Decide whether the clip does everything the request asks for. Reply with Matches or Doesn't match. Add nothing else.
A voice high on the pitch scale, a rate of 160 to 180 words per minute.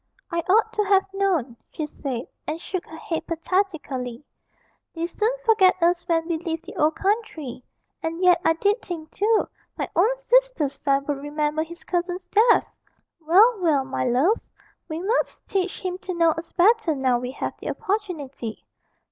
Matches